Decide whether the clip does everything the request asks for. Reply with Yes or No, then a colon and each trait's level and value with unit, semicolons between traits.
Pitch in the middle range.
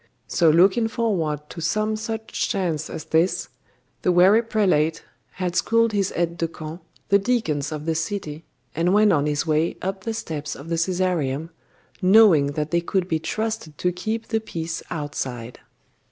Yes: medium, 170 Hz